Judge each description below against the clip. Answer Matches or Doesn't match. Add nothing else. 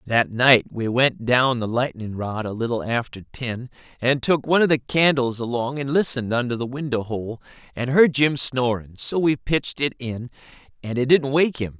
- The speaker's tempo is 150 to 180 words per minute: Doesn't match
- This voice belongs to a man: Matches